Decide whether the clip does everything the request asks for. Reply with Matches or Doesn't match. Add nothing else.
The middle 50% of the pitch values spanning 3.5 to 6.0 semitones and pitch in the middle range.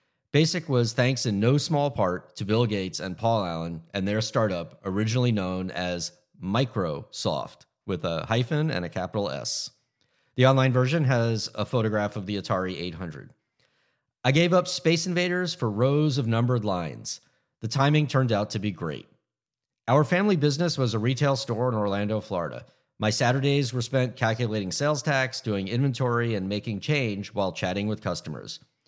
Doesn't match